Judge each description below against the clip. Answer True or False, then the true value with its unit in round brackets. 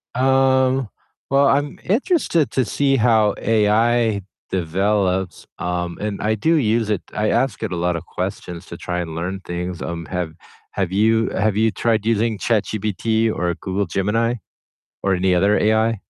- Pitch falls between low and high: False (105 Hz)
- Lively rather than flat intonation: False (4.0 semitones)